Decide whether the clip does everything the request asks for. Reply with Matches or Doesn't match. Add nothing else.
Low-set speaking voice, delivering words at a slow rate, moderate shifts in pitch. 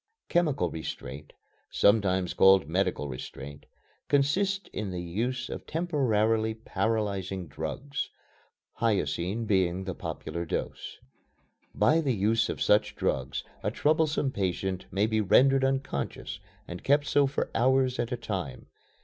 Doesn't match